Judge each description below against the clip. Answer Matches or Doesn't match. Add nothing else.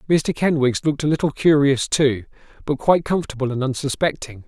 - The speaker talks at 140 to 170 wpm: Matches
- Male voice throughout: Matches